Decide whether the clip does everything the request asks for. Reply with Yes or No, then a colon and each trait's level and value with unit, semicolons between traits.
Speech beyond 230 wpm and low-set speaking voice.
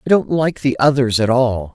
Yes: fast, 240 wpm; low, 130 Hz